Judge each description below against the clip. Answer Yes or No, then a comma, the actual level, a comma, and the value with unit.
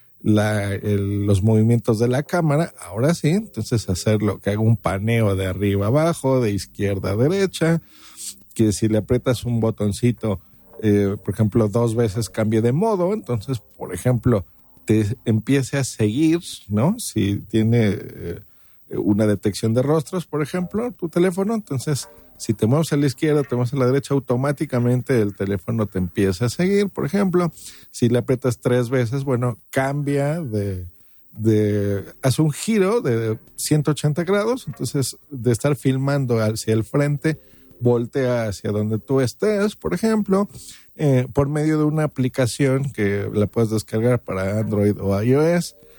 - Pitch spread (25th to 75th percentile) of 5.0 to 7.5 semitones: Yes, wide, 5.5 semitones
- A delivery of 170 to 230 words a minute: No, average, 155 wpm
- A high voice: No, low, 120 Hz